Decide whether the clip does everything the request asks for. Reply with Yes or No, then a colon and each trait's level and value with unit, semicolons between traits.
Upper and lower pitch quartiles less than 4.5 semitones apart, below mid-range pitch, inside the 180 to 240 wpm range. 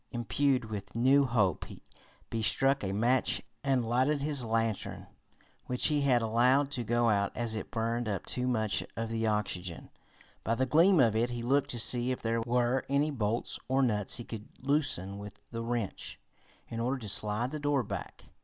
Yes: average, 3.1 semitones; low, 120 Hz; average, 185 wpm